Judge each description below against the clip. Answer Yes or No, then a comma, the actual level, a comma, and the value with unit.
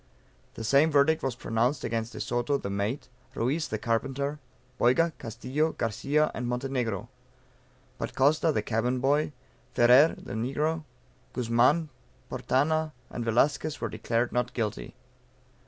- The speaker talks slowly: Yes, slow, 130 wpm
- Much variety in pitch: No, average, 4.3 semitones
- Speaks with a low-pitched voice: Yes, low, 125 Hz